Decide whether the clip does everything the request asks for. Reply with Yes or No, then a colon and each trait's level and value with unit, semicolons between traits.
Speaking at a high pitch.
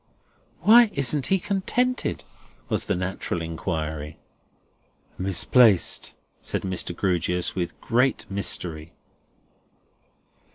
No: very low, 95 Hz